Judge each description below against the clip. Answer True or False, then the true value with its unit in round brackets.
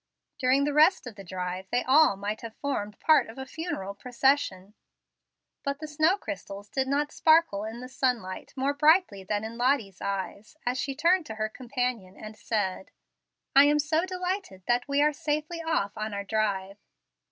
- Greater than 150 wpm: True (175 wpm)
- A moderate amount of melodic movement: False (6.6 semitones)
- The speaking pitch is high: True (250 Hz)